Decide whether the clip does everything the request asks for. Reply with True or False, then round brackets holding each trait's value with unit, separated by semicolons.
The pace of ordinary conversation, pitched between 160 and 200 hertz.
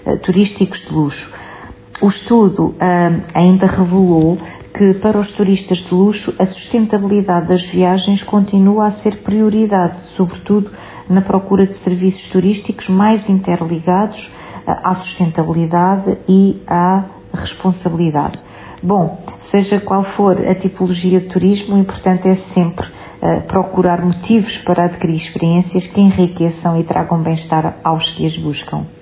True (130 wpm; 185 Hz)